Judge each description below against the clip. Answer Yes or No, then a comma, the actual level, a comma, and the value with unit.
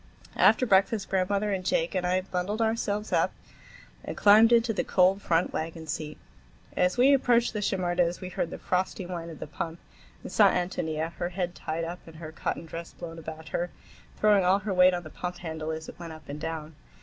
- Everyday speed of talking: No, fast, 210 wpm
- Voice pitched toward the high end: No, medium, 180 Hz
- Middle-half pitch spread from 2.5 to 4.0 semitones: Yes, average, 3.2 semitones